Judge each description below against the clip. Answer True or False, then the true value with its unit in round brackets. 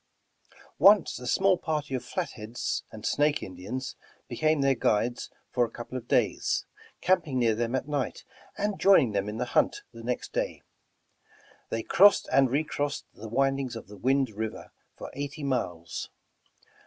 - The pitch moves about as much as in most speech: True (4.4 semitones)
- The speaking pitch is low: True (130 Hz)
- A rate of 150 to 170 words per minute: True (155 wpm)